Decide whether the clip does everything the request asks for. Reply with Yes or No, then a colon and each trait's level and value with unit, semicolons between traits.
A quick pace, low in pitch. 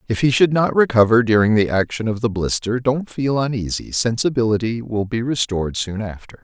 No: average, 185 wpm; low, 115 Hz